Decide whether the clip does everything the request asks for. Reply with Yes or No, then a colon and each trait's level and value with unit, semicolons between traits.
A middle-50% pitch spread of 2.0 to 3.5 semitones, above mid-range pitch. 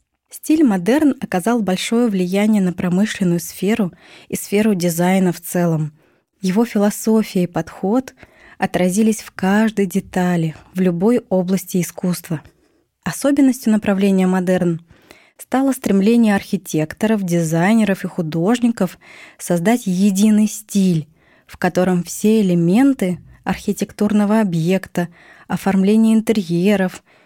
Yes: average, 3.2 semitones; high, 195 Hz